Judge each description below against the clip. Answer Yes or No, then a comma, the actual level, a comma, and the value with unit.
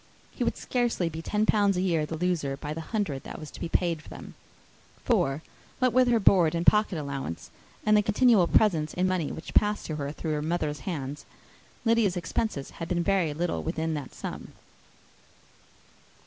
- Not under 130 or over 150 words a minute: No, average, 185 wpm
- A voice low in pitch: No, medium, 170 Hz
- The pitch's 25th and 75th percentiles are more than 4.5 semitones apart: Yes, average, 5.1 semitones